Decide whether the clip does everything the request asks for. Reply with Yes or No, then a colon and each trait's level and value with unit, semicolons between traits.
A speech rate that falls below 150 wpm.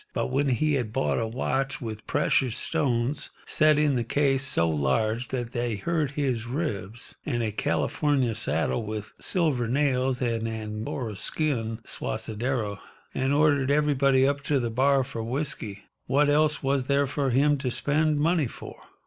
No: average, 155 wpm